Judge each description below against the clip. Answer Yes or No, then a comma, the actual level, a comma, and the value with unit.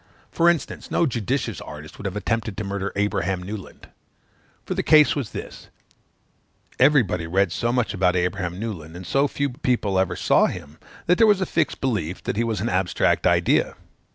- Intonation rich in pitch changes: Yes, wide, 6.0 semitones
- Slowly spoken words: No, average, 180 wpm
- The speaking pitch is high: No, low, 105 Hz